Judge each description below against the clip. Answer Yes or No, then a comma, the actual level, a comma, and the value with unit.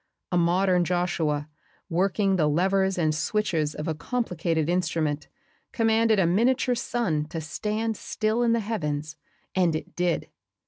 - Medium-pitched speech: Yes, medium, 180 Hz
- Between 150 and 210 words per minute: No, average, 140 wpm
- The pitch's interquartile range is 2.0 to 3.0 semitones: No, average, 5.3 semitones